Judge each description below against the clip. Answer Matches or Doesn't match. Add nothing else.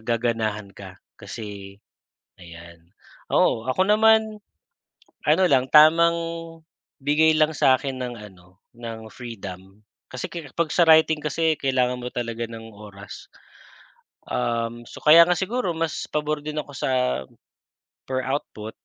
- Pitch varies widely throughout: Matches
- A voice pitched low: Matches